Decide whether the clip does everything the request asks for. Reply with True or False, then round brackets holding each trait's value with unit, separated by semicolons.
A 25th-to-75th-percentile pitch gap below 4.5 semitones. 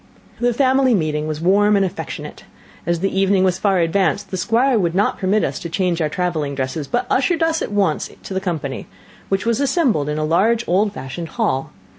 False (5.2 semitones)